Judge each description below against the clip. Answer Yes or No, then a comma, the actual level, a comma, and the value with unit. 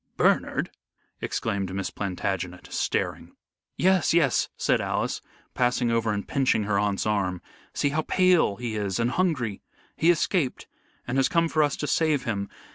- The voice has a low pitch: Yes, low, 120 Hz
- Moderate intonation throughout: No, wide, 7.4 semitones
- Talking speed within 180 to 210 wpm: No, average, 155 wpm